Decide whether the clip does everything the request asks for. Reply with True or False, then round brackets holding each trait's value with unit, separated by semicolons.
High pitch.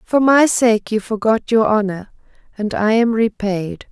True (220 Hz)